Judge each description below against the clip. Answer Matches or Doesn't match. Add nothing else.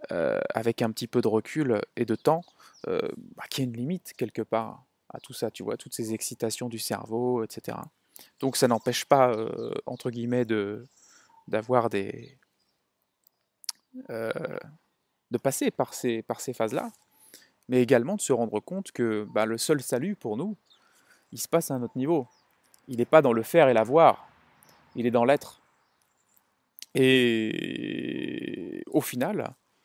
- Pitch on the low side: Matches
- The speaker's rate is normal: Matches